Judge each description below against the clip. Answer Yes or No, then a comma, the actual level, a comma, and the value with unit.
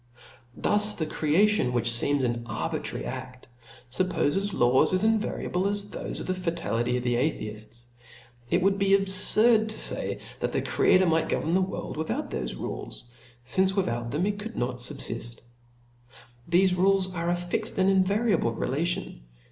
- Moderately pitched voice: Yes, medium, 175 Hz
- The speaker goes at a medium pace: Yes, average, 155 wpm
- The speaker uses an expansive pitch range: Yes, wide, 7.8 semitones